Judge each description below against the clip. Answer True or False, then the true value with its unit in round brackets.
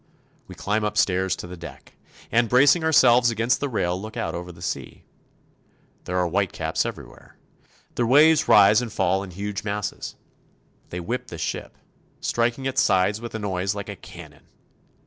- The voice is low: True (105 Hz)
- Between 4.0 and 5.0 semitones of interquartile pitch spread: True (4.4 semitones)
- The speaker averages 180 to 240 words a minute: False (170 wpm)